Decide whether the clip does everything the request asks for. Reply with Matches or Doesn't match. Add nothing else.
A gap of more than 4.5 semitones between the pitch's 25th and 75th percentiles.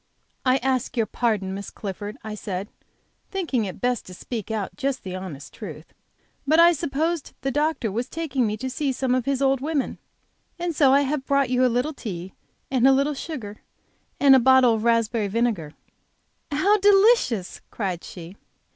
Matches